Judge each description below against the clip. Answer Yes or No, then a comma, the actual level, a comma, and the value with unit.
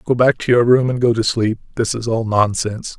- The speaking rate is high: Yes, fast, 260 wpm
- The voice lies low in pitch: Yes, low, 115 Hz